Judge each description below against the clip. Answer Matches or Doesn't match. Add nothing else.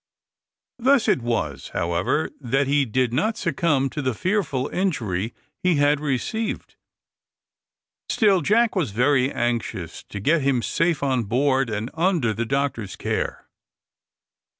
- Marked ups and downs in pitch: Matches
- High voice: Doesn't match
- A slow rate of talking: Matches